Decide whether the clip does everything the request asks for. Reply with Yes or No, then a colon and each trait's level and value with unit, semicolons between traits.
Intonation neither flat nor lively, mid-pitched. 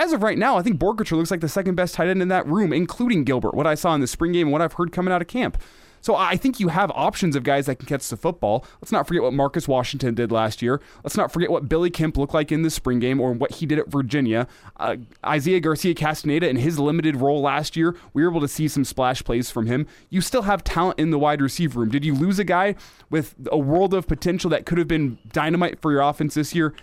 Yes: average, 3.9 semitones; medium, 155 Hz